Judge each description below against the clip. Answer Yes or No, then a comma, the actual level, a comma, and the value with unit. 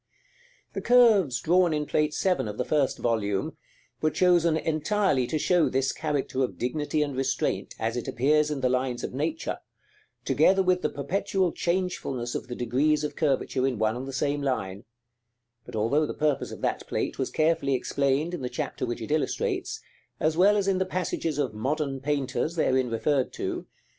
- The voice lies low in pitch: No, medium, 145 Hz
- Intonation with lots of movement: No, average, 4.3 semitones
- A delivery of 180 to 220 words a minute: Yes, average, 185 wpm